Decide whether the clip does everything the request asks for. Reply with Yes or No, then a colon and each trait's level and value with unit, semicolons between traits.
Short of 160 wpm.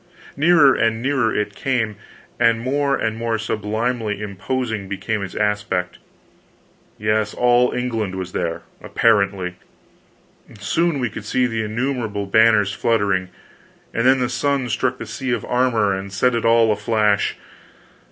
Yes: average, 140 wpm